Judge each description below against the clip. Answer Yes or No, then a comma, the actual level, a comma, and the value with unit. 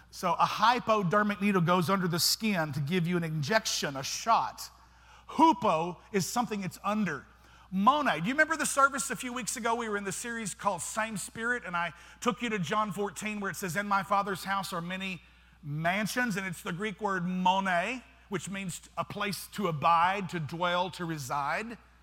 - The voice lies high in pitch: Yes, high, 195 Hz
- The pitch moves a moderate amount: Yes, average, 4.0 semitones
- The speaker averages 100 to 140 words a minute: No, average, 195 wpm